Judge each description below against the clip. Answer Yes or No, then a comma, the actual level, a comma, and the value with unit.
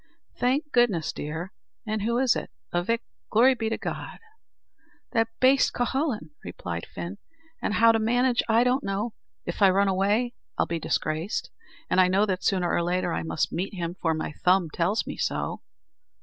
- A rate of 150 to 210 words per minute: Yes, average, 175 wpm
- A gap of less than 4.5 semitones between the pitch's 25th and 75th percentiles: No, wide, 5.4 semitones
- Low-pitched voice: No, high, 200 Hz